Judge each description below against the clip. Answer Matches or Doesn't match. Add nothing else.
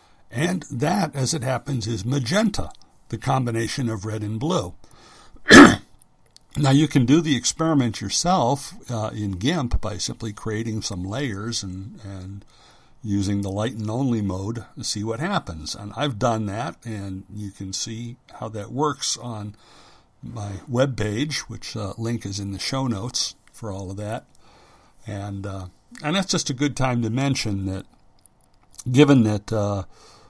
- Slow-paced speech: Doesn't match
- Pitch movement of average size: Matches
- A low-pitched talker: Matches